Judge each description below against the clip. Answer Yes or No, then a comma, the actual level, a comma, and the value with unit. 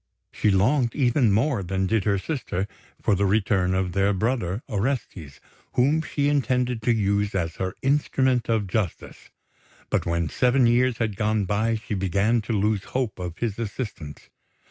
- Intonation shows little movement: No, average, 4.3 semitones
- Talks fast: No, average, 165 wpm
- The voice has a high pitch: No, low, 110 Hz